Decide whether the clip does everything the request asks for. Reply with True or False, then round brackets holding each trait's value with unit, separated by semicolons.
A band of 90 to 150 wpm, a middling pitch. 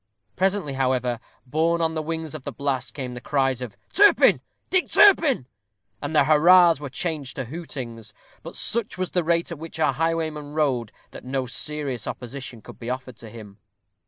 False (180 wpm; 145 Hz)